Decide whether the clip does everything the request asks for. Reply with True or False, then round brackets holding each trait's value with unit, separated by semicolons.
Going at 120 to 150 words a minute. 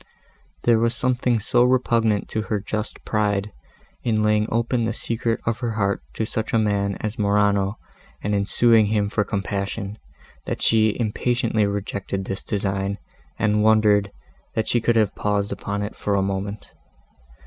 False (165 wpm)